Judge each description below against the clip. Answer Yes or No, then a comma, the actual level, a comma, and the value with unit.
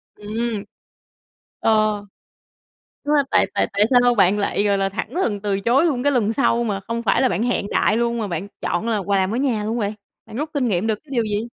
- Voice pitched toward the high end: Yes, high, 220 Hz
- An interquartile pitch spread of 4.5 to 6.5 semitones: No, average, 3.2 semitones